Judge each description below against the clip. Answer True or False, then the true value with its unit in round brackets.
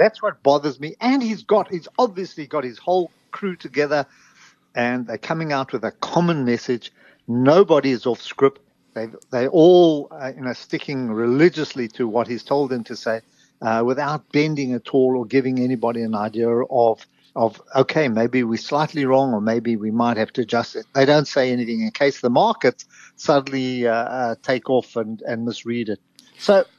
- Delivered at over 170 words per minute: True (190 wpm)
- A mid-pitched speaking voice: False (130 Hz)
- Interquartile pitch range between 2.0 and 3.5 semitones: False (4.2 semitones)